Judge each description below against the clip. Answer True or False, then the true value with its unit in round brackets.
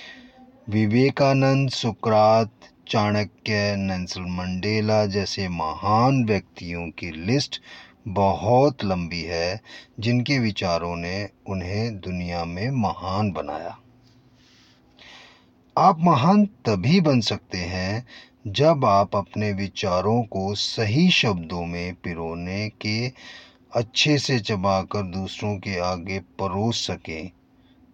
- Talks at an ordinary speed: False (95 wpm)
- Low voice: True (105 Hz)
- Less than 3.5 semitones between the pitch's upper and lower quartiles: False (5.1 semitones)